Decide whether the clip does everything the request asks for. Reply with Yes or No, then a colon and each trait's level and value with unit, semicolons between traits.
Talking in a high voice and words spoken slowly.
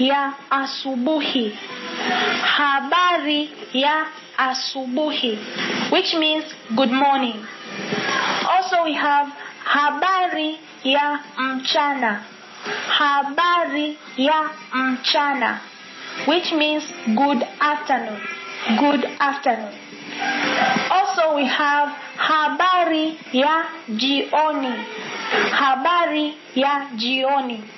Yes: very high, 290 Hz; slow, 70 wpm